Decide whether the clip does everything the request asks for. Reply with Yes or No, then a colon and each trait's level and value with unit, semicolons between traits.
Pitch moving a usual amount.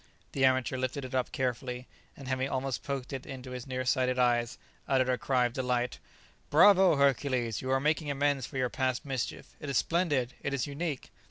No: narrow, 1.7 semitones